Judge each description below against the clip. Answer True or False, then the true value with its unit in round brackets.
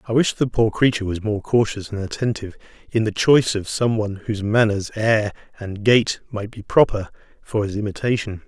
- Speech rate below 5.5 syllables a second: False (5.6 syllables/s)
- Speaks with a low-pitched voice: True (110 Hz)